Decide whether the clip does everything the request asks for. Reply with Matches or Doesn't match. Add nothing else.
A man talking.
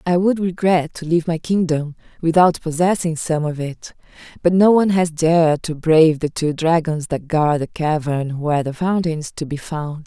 Doesn't match